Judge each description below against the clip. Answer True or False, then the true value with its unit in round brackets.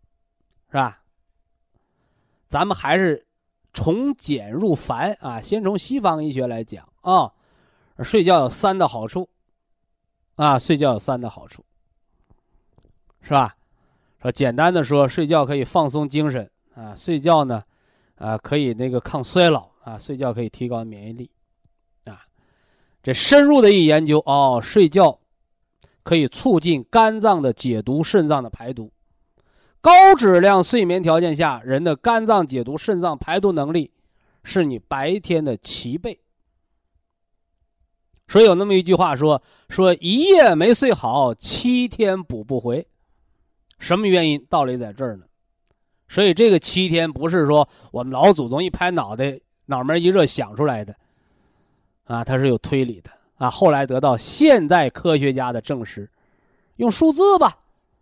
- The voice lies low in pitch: False (145 Hz)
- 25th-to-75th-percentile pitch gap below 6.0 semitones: False (7.4 semitones)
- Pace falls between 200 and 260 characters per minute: True (210 characters per minute)